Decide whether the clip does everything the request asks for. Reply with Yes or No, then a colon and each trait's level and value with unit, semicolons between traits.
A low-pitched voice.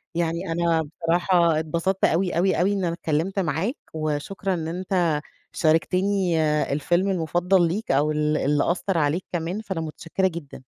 No: medium, 170 Hz